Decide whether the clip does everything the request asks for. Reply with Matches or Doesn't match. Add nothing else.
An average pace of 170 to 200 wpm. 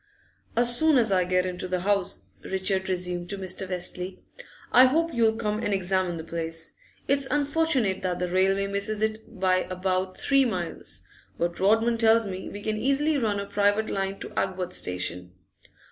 Matches